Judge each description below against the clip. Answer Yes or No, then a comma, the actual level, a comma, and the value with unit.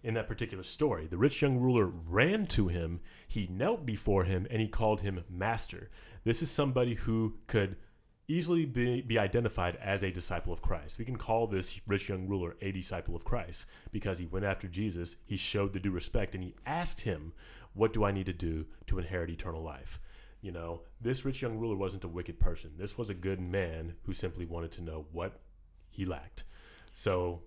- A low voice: Yes, very low, 95 Hz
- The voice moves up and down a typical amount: Yes, average, 4.2 semitones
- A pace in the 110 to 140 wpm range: No, fast, 205 wpm